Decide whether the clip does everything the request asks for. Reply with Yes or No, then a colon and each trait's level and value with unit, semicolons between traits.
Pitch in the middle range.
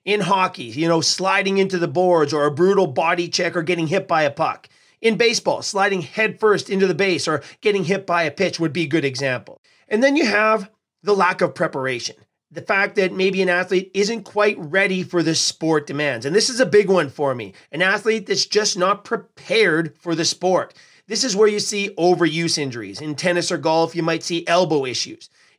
Yes: medium, 180 Hz